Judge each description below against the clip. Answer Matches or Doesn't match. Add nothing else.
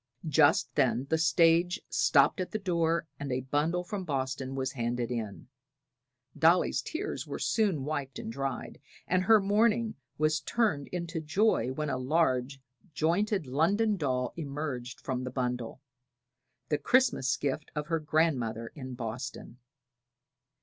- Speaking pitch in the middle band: Matches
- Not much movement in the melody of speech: Doesn't match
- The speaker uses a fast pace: Doesn't match